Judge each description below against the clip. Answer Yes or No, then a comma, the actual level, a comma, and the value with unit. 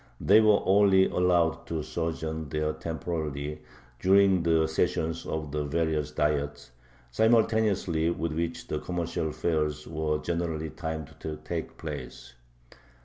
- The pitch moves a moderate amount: No, narrow, 2.1 semitones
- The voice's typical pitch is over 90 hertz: No, very low, 80 Hz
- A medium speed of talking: No, slow, 125 wpm